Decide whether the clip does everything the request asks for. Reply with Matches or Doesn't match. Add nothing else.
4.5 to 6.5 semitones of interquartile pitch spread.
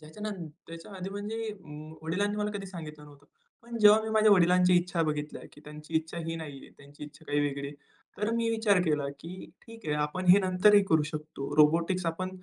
Matches